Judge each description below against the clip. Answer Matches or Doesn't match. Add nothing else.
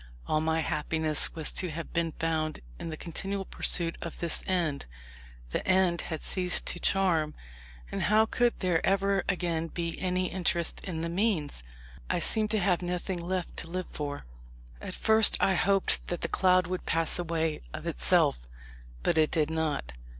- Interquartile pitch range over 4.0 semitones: Doesn't match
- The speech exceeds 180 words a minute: Doesn't match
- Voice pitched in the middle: Matches